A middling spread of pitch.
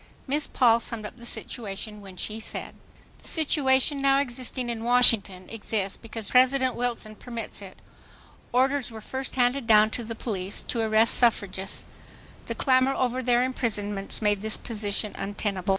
Yes: average, 3.4 semitones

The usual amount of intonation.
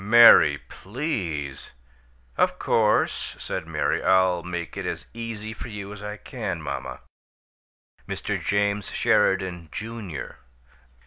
Yes: average, 4.5 semitones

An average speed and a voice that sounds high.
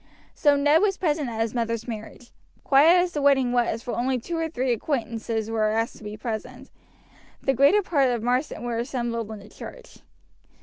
Yes: average, 190 wpm; high, 245 Hz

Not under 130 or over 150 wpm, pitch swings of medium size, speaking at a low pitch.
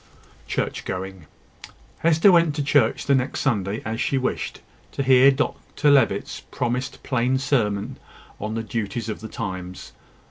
Yes: average, 145 wpm; average, 5.0 semitones; low, 120 Hz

